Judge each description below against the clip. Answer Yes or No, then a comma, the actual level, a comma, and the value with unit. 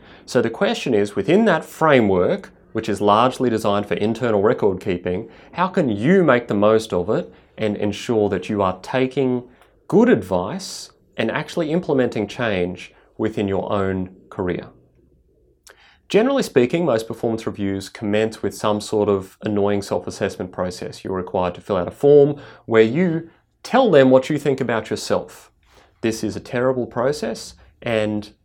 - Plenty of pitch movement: No, average, 4.0 semitones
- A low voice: Yes, low, 110 Hz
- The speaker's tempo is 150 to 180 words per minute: Yes, average, 160 wpm